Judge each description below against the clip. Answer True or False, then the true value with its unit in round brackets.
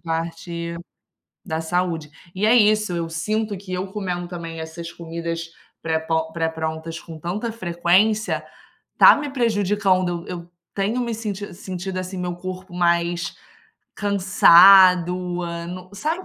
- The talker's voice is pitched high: False (180 Hz)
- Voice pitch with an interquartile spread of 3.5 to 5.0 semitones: False (3.1 semitones)